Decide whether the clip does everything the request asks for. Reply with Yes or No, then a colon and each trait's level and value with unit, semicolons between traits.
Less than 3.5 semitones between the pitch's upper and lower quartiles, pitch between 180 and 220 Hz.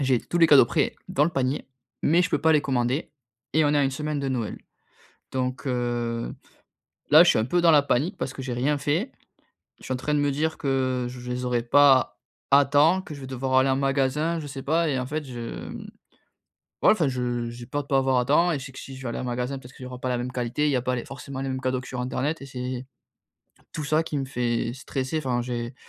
No: average, 2.7 semitones; low, 135 Hz